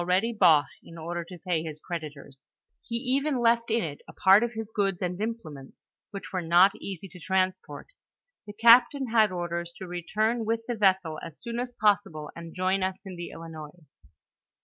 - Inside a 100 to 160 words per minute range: No, average, 185 wpm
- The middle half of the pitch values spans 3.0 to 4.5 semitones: No, average, 4.9 semitones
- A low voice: No, medium, 185 Hz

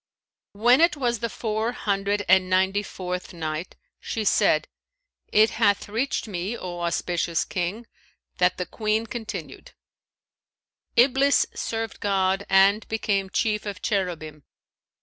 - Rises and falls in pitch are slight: No, average, 3.4 semitones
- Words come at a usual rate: No, slow, 125 wpm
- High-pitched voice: Yes, high, 200 Hz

